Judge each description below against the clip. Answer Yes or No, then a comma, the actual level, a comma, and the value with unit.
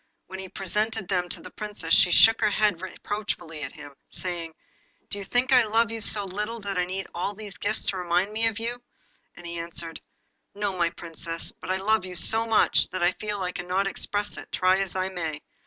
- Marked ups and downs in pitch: No, average, 3.1 semitones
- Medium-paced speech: No, fast, 220 wpm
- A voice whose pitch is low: No, high, 195 Hz